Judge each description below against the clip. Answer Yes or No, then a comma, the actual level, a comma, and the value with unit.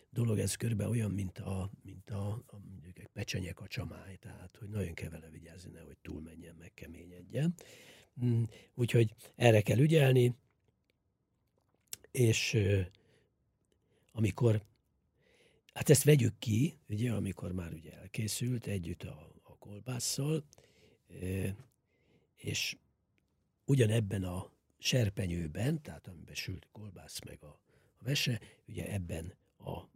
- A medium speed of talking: No, slow, 115 wpm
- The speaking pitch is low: Yes, low, 105 Hz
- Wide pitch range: No, average, 4.7 semitones